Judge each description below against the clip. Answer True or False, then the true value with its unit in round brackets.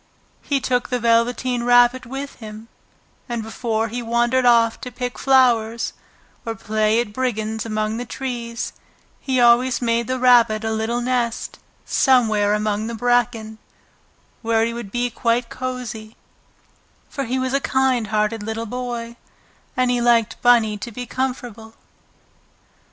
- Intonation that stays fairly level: True (2.0 semitones)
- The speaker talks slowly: False (145 wpm)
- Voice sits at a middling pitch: False (235 Hz)